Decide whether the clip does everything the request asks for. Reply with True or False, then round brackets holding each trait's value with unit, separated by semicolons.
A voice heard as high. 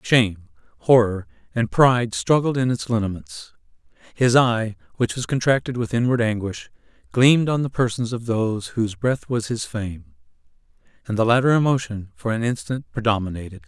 False (110 Hz)